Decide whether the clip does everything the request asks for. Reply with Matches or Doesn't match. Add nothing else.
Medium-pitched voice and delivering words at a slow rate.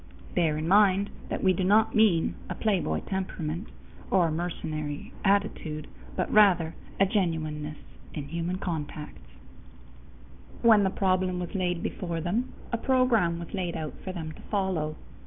Doesn't match